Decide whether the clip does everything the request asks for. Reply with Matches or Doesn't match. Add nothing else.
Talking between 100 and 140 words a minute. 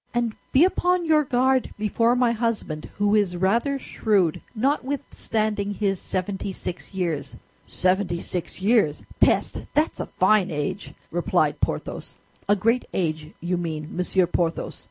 Matches